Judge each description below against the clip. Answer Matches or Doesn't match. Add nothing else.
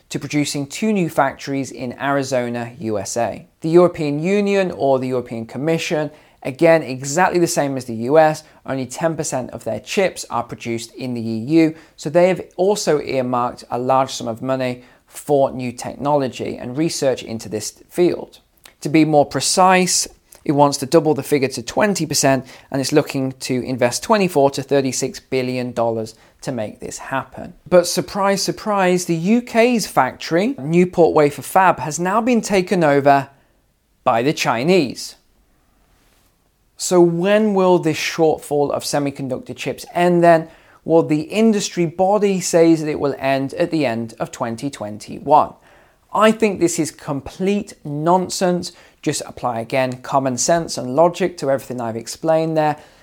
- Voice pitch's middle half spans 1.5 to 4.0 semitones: Doesn't match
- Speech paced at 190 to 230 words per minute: Doesn't match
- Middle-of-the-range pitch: Matches